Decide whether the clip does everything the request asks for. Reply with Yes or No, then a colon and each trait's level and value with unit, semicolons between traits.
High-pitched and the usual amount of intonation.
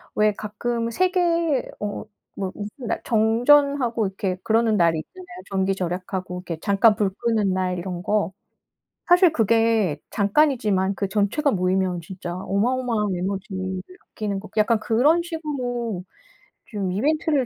Yes: high, 210 Hz; average, 4.4 semitones